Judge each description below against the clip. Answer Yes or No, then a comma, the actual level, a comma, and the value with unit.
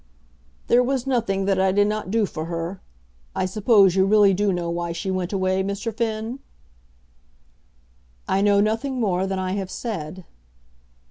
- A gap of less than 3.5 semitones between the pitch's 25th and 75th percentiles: Yes, narrow, 2.6 semitones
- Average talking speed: Yes, average, 160 wpm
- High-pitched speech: Yes, high, 195 Hz